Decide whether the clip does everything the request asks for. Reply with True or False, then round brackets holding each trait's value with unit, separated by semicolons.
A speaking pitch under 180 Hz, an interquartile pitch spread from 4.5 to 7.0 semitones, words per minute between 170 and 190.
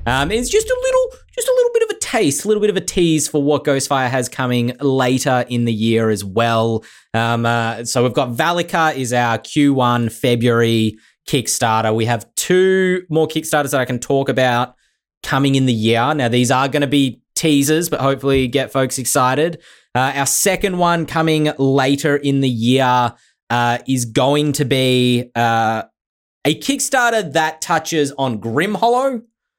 True (135 Hz; 4.8 semitones; 180 wpm)